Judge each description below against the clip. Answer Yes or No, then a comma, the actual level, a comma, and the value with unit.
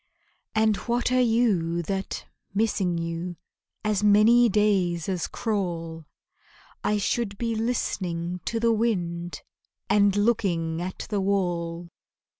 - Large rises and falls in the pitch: No, average, 4.3 semitones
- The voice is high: Yes, high, 195 Hz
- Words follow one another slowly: Yes, slow, 115 wpm